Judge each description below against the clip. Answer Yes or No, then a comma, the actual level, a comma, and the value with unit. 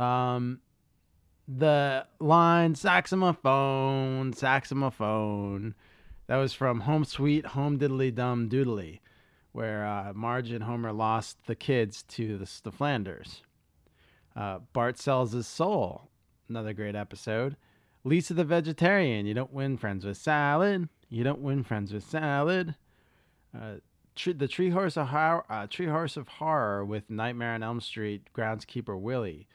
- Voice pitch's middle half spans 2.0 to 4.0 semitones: No, average, 4.8 semitones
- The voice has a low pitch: Yes, low, 125 Hz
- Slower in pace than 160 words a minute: Yes, average, 140 wpm